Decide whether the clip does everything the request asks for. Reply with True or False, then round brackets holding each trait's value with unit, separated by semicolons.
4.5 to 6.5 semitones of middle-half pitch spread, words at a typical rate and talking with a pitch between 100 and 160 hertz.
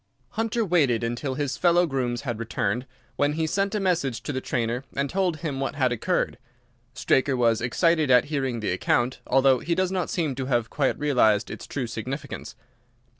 True (4.9 semitones; 185 wpm; 135 Hz)